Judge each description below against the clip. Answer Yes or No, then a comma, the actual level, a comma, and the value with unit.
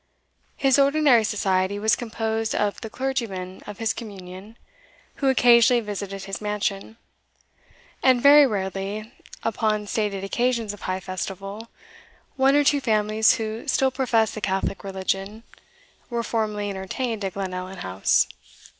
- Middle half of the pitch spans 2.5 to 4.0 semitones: Yes, average, 3.3 semitones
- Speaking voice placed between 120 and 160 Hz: No, high, 215 Hz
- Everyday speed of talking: No, slow, 130 wpm